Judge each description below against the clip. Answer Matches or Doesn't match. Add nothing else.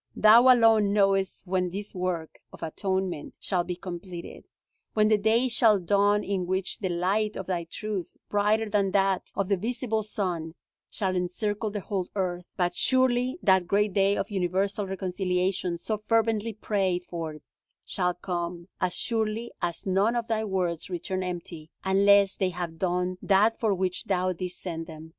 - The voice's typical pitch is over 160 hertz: Matches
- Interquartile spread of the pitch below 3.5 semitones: Matches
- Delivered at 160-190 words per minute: Matches